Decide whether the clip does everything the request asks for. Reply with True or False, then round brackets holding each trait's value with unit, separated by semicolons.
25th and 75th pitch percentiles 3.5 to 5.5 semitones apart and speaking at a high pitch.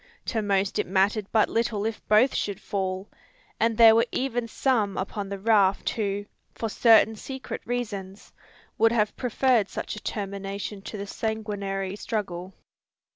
False (2.4 semitones; 210 Hz)